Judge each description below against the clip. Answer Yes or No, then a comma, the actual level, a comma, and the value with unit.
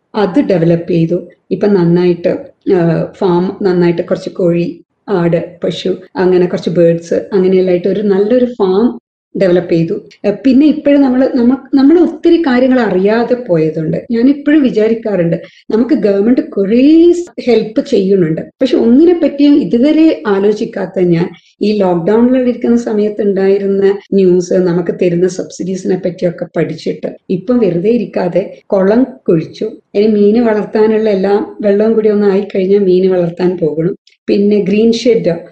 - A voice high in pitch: Yes, high, 200 Hz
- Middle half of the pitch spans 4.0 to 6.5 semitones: Yes, average, 4.6 semitones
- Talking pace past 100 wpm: Yes, average, 120 wpm